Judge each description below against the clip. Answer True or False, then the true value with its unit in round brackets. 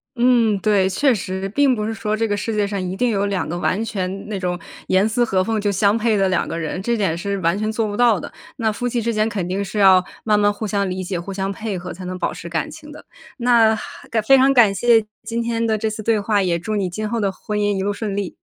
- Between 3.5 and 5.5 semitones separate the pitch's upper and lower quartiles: False (2.9 semitones)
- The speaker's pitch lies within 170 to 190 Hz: False (205 Hz)